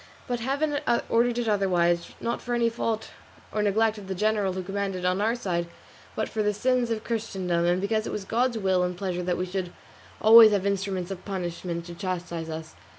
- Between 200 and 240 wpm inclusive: Yes, fast, 205 wpm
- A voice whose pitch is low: No, high, 195 Hz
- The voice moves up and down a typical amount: Yes, average, 3.8 semitones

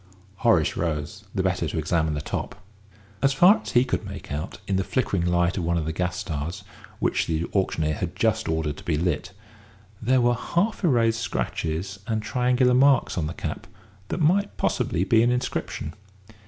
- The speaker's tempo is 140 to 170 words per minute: No, average, 185 wpm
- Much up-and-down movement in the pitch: Yes, wide, 7.2 semitones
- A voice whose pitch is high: No, very low, 95 Hz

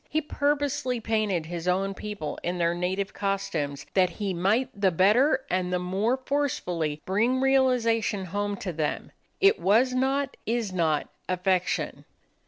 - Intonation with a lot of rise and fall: Yes, wide, 5.9 semitones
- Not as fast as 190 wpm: Yes, average, 145 wpm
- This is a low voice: No, high, 200 Hz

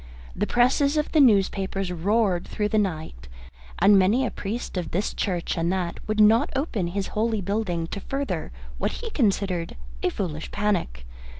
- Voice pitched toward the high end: Yes, high, 200 Hz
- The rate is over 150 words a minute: Yes, average, 170 wpm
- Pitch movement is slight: No, average, 4.1 semitones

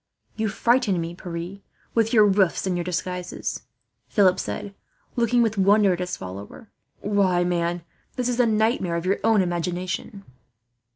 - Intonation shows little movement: No, average, 3.7 semitones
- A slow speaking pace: No, average, 155 wpm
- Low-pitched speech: No, high, 190 Hz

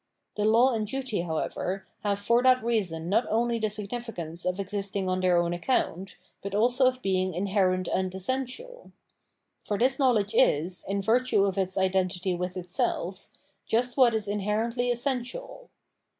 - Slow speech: No, average, 160 wpm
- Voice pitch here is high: Yes, high, 205 Hz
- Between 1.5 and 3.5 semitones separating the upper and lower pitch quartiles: No, average, 4.6 semitones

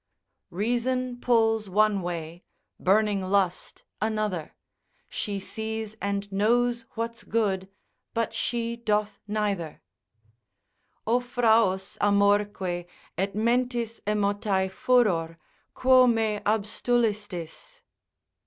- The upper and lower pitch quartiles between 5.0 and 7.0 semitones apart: No, average, 2.9 semitones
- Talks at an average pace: No, slow, 90 wpm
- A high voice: Yes, high, 210 Hz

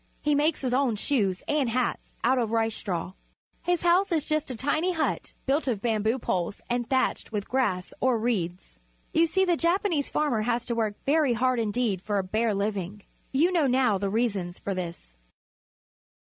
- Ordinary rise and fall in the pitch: No, wide, 5.9 semitones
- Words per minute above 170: Yes, average, 185 wpm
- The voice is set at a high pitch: Yes, high, 240 Hz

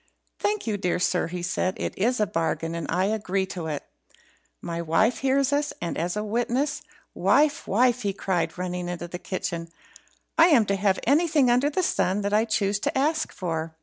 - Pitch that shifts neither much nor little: No, wide, 6.1 semitones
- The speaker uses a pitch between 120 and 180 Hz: No, high, 200 Hz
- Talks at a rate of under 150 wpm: No, average, 185 wpm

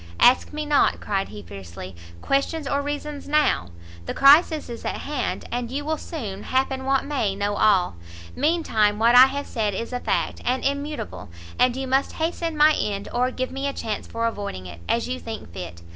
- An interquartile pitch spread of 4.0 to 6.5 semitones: Yes, wide, 5.5 semitones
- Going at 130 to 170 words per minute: No, average, 200 wpm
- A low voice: No, very high, 255 Hz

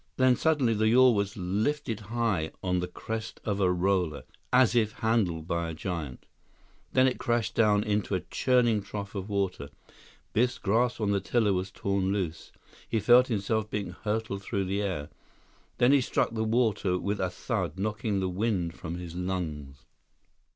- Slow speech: No, average, 170 wpm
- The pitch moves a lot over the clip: No, average, 3.7 semitones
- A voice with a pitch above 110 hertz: No, low, 100 Hz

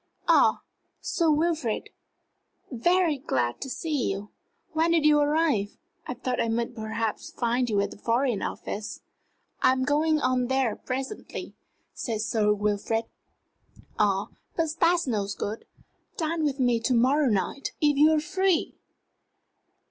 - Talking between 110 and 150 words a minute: Yes, average, 140 wpm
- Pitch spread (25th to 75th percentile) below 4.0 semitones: No, wide, 5.5 semitones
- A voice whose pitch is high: Yes, very high, 255 Hz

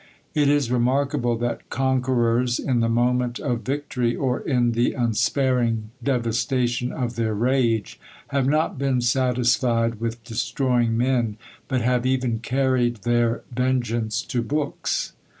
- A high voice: No, low, 120 Hz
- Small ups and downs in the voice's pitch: Yes, narrow, 1.8 semitones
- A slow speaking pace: Yes, slow, 130 wpm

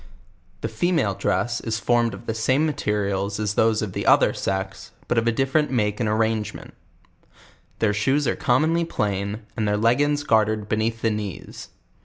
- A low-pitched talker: Yes, low, 110 Hz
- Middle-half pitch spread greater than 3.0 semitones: No, average, 2.7 semitones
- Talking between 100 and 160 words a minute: No, average, 170 wpm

